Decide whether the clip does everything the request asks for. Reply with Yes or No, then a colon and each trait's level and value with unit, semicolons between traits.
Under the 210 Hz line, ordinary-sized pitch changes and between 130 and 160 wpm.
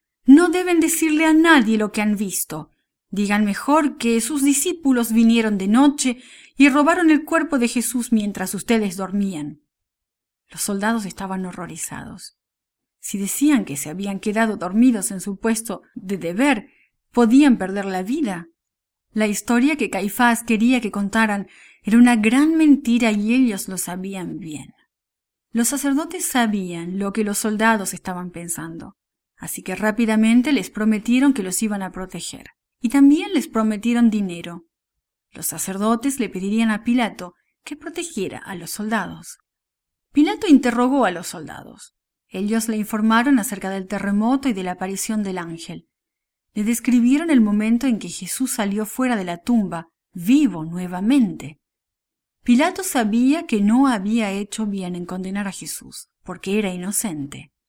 No: high, 220 Hz; average, 4.9 semitones; average, 150 wpm